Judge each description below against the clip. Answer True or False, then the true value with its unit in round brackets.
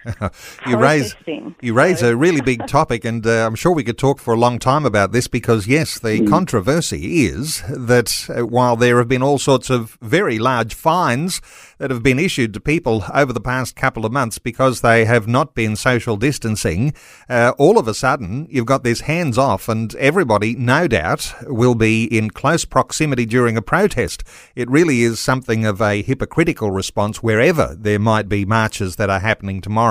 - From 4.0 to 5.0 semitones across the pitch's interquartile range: False (3.2 semitones)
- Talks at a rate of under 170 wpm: False (190 wpm)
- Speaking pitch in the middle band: False (120 Hz)